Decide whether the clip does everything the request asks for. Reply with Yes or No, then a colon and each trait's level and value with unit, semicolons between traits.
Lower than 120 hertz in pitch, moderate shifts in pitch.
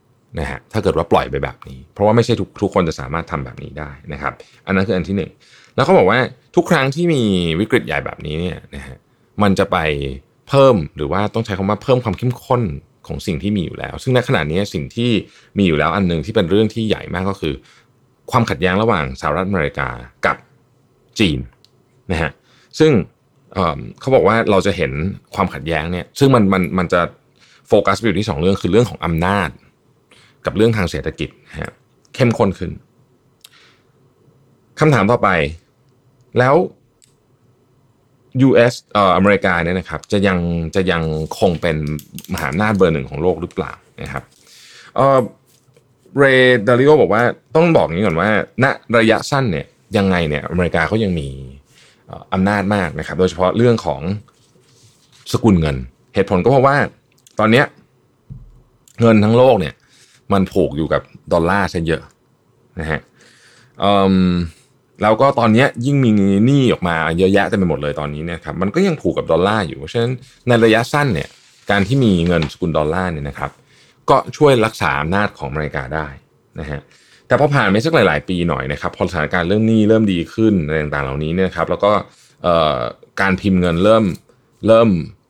No: low, 100 Hz; wide, 6.7 semitones